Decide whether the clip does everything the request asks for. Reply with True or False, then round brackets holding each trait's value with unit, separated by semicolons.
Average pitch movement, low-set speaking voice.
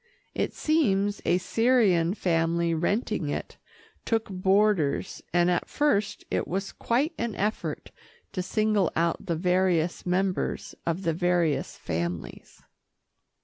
False (3.9 semitones; 185 Hz)